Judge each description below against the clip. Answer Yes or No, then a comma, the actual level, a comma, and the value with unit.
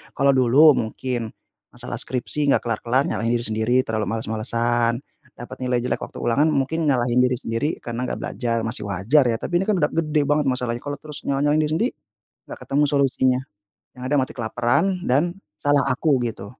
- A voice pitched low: Yes, low, 130 Hz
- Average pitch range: Yes, average, 3.8 semitones